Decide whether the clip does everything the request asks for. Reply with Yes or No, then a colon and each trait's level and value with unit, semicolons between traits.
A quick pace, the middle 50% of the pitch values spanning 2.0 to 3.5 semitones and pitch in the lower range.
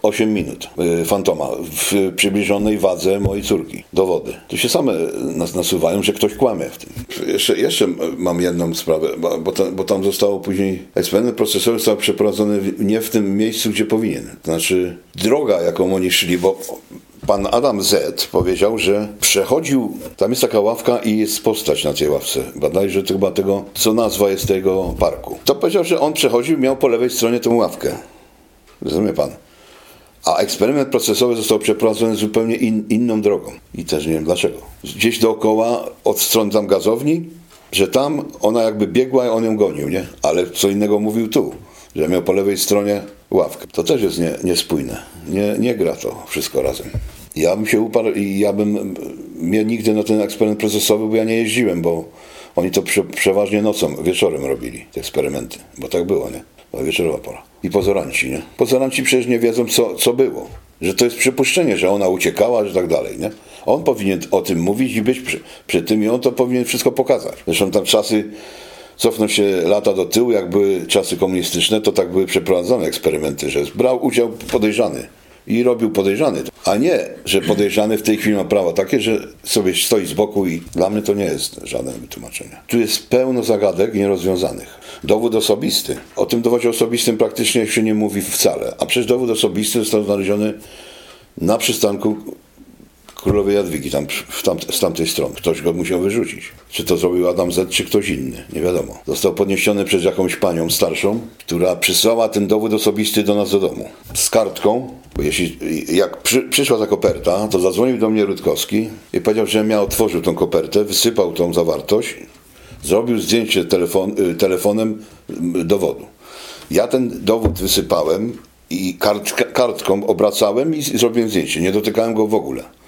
Yes: fast, 180 wpm; average, 2.7 semitones; low, 105 Hz